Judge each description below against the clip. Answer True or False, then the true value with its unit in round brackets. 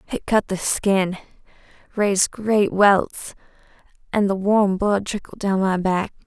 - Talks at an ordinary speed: True (145 wpm)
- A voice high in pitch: True (200 Hz)